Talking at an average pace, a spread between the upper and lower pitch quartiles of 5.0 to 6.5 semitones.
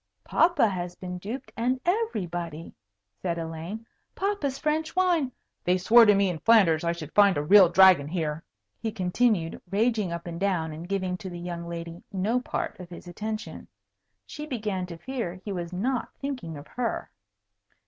Yes: average, 175 wpm; average, 5.3 semitones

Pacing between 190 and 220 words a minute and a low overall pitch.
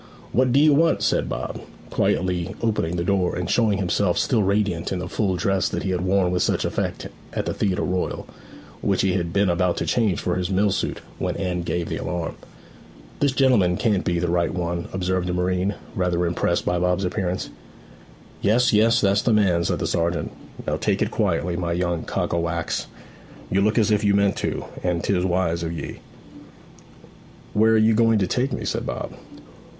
Yes: average, 195 wpm; very low, 95 Hz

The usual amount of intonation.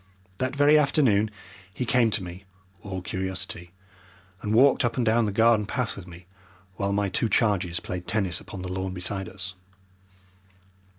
Yes: average, 3.8 semitones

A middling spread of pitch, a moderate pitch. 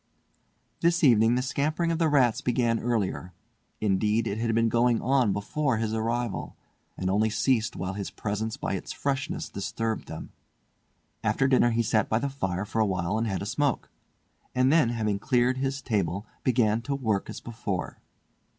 No: average, 3.6 semitones; low, 115 Hz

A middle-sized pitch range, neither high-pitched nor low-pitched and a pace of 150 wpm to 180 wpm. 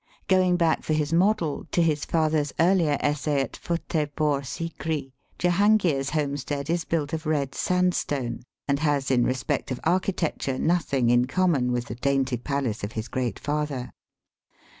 Yes: average, 3.7 semitones; medium, 150 Hz; average, 155 wpm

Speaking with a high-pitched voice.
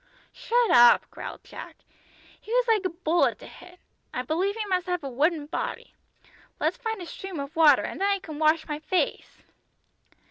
Yes: very high, 350 Hz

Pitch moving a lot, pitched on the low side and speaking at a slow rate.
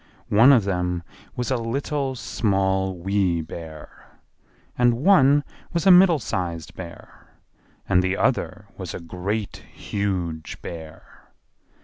Yes: wide, 6.0 semitones; very low, 95 Hz; slow, 120 wpm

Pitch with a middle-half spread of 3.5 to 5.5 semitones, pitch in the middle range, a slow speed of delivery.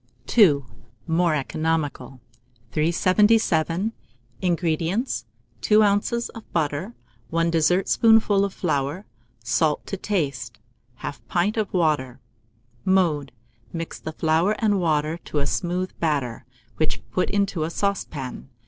Yes: average, 4.6 semitones; medium, 165 Hz; slow, 110 wpm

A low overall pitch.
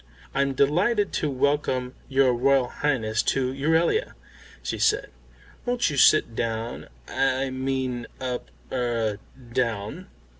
Yes: low, 130 Hz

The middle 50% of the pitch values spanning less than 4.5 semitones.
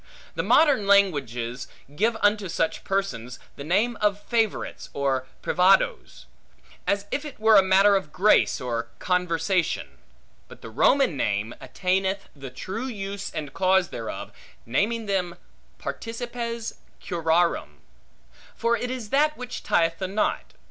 No: average, 5.3 semitones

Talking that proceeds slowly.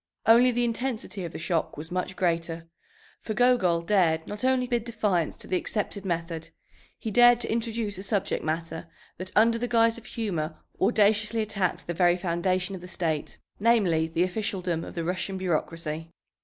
No: average, 175 wpm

